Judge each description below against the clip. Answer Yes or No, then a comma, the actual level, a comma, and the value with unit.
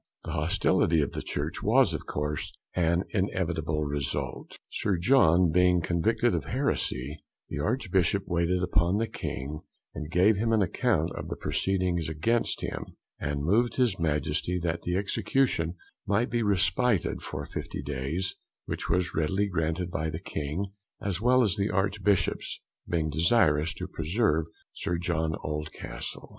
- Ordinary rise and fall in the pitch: Yes, average, 4.0 semitones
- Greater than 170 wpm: No, average, 150 wpm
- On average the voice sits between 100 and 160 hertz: No, very low, 85 Hz